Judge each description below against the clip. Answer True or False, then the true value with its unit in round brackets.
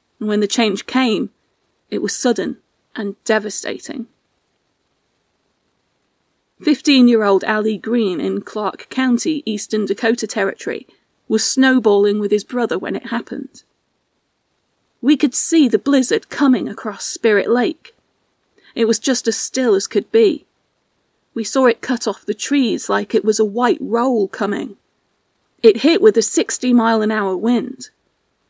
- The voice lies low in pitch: False (235 Hz)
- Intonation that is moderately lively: True (3.6 semitones)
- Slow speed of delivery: False (145 wpm)